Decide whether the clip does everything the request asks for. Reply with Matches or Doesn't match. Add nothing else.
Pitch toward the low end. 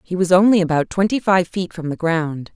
Doesn't match